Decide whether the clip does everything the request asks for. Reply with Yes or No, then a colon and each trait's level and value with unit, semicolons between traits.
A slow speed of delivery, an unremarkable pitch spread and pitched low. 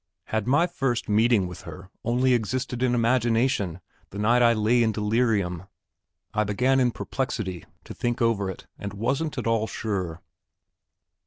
No: average, 155 wpm; average, 3.4 semitones; low, 115 Hz